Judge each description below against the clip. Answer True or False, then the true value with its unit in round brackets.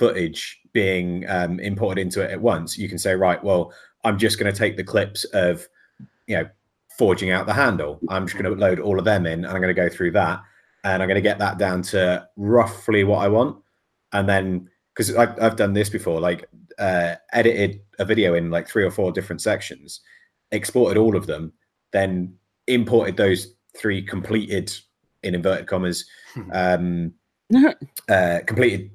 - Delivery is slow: False (185 wpm)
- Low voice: True (95 Hz)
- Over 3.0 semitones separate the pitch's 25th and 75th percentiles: False (2.7 semitones)